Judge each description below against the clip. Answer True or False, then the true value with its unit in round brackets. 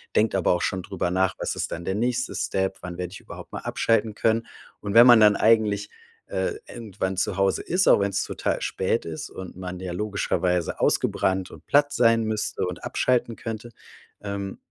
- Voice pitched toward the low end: True (100 Hz)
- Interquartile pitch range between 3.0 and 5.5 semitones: True (3.4 semitones)